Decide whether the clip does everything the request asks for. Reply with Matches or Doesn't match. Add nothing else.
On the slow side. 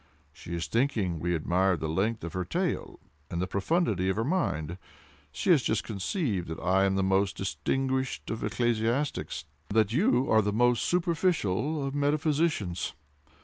Doesn't match